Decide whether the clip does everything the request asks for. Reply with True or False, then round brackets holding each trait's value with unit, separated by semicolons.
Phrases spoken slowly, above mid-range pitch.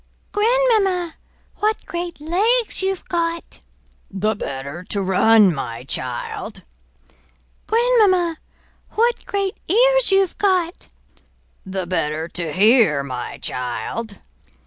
True (100 wpm; 335 Hz)